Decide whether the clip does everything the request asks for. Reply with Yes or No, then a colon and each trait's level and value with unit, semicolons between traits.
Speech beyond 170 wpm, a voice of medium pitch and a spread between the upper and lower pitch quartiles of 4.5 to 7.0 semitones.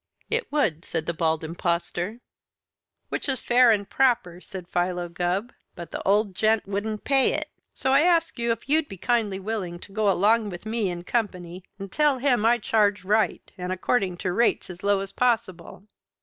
No: average, 195 wpm; high, 205 Hz; average, 4.8 semitones